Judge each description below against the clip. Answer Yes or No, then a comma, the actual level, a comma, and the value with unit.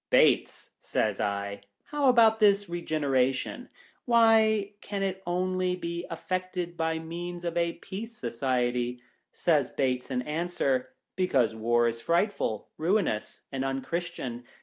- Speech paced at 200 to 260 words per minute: No, average, 145 wpm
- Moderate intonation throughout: No, wide, 6.8 semitones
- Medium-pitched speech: Yes, medium, 170 Hz